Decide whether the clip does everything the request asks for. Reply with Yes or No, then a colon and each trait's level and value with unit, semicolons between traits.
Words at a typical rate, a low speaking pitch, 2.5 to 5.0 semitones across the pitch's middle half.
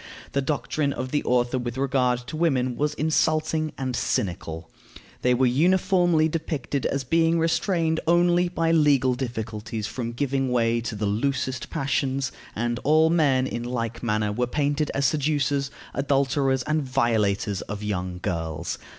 Yes: average, 150 wpm; low, 130 Hz; average, 4.5 semitones